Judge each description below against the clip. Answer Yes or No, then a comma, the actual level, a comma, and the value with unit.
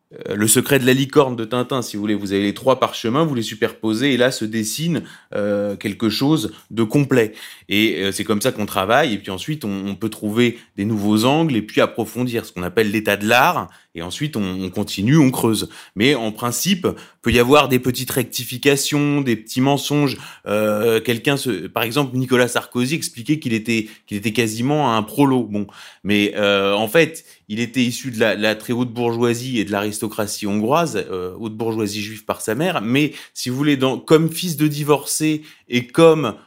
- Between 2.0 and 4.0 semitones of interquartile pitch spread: No, average, 4.4 semitones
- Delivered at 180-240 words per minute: Yes, average, 205 wpm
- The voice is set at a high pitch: No, low, 120 Hz